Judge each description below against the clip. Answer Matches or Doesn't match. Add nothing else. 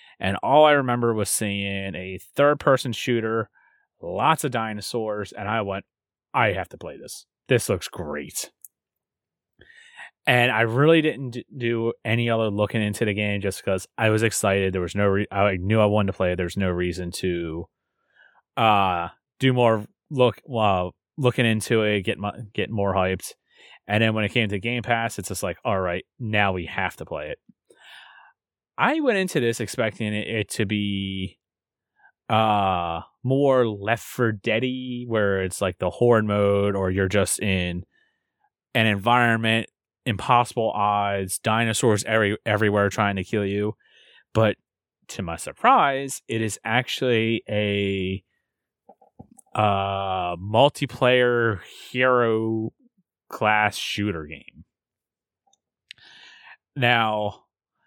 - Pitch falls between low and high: Doesn't match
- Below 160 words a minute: Matches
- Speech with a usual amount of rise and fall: Matches